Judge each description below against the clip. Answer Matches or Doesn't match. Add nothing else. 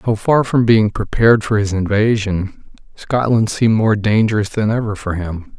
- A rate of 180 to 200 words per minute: Doesn't match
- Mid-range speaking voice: Doesn't match